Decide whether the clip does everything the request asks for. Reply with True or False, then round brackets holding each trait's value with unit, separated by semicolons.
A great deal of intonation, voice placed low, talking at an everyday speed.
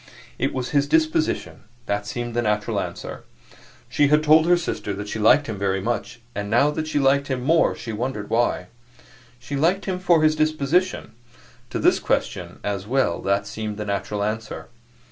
True (6.6 semitones; 125 Hz; 185 wpm)